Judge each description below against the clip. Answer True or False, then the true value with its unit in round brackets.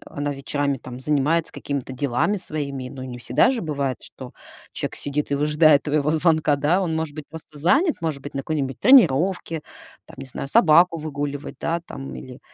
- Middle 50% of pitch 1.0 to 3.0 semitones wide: True (2.7 semitones)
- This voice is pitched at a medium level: True (150 Hz)